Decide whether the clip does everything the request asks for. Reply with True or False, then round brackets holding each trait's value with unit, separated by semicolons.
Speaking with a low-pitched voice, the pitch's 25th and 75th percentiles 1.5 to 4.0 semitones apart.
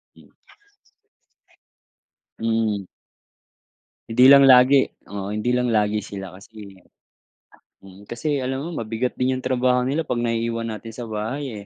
True (115 Hz; 3.3 semitones)